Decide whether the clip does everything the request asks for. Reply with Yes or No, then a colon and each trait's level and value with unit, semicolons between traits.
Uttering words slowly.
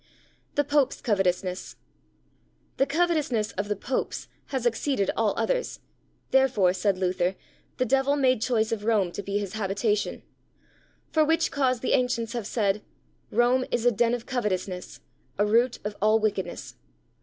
No: average, 150 wpm